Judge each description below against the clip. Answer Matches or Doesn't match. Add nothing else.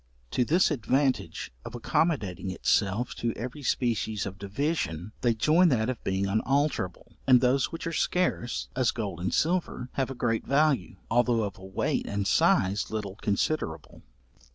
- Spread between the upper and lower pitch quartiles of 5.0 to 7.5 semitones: Matches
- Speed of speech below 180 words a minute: Matches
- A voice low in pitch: Matches